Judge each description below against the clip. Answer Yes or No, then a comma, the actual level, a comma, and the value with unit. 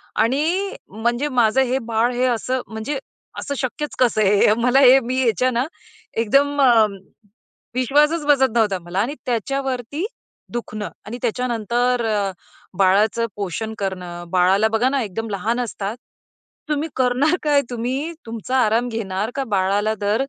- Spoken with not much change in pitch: No, average, 3.6 semitones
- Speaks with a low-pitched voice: No, high, 235 Hz